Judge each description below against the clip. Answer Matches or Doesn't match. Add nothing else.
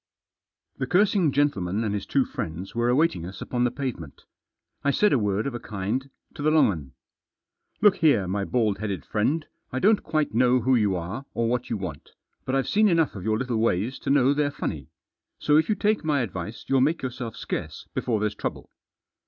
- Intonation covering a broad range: Matches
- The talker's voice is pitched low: Matches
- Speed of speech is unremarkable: Doesn't match